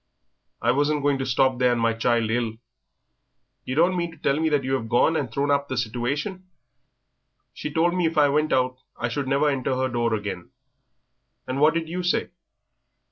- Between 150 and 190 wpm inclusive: No, average, 200 wpm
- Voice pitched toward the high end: No, low, 135 Hz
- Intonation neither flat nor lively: Yes, average, 3.9 semitones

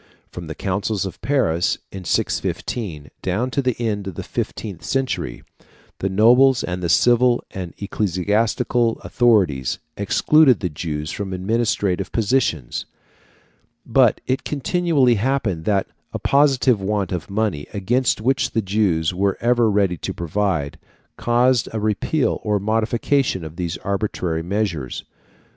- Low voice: Yes, low, 105 Hz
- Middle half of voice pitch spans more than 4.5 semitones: Yes, average, 5.0 semitones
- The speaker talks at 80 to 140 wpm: Yes, slow, 135 wpm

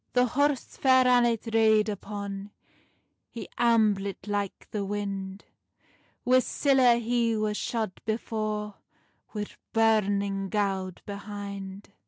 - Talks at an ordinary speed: No, slow, 105 wpm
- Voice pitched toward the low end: No, high, 210 Hz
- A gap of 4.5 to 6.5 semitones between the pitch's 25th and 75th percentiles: No, narrow, 2.6 semitones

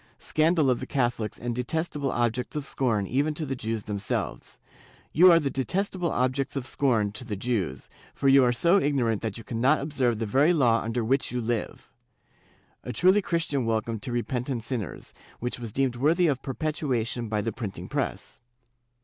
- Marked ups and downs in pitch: No, average, 3.9 semitones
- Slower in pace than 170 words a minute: No, average, 185 wpm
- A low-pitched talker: Yes, low, 125 Hz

